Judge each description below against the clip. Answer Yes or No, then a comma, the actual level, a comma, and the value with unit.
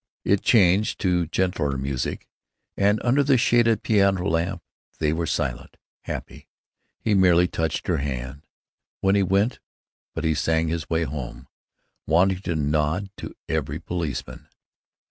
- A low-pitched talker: Yes, very low, 85 Hz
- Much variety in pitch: No, average, 4.4 semitones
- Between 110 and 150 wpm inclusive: Yes, average, 140 wpm